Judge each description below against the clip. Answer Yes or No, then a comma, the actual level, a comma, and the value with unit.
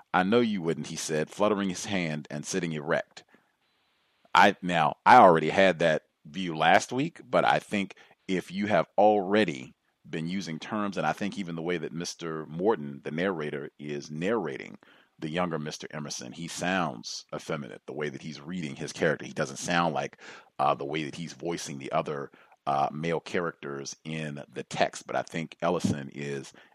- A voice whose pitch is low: Yes, very low, 80 Hz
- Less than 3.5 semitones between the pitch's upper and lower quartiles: No, average, 4.1 semitones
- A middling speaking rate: Yes, average, 180 wpm